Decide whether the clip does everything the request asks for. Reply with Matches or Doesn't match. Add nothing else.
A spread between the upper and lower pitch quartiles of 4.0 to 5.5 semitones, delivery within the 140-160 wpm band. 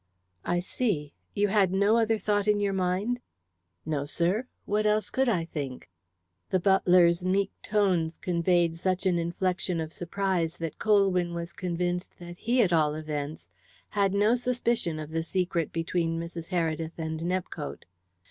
Doesn't match